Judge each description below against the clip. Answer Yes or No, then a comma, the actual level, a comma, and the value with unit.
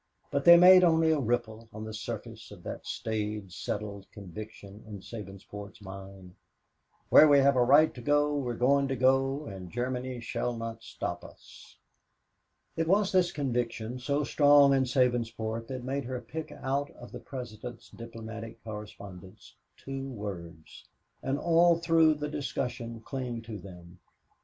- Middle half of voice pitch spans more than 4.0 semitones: Yes, average, 4.5 semitones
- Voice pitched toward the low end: Yes, low, 120 Hz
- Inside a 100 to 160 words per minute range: Yes, average, 150 wpm